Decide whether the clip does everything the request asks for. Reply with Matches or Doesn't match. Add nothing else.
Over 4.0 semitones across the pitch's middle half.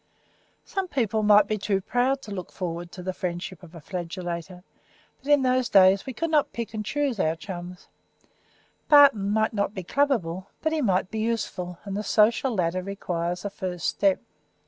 Matches